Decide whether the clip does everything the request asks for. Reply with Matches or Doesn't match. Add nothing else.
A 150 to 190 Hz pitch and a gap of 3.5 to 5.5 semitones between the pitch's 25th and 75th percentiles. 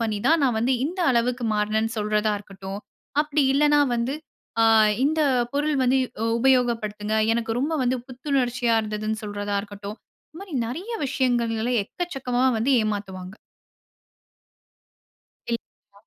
Doesn't match